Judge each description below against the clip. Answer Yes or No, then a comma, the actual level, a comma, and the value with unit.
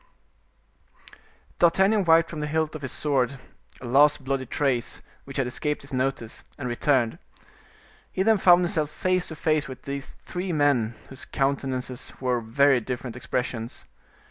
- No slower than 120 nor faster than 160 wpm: Yes, average, 150 wpm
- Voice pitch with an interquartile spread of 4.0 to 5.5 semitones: No, average, 3.6 semitones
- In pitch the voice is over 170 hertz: No, medium, 140 Hz